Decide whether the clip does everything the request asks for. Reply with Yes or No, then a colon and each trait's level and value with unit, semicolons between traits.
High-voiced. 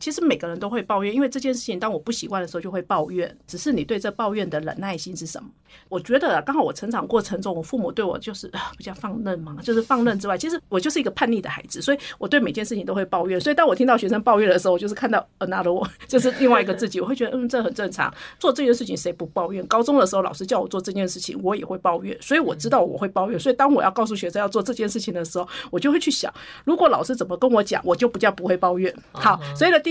Yes: high, 215 Hz